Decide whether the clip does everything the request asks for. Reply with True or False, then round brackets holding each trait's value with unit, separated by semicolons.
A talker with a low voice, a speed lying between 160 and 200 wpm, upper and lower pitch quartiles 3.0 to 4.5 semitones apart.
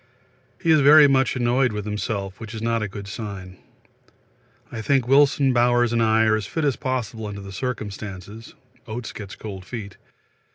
True (110 Hz; 175 wpm; 3.7 semitones)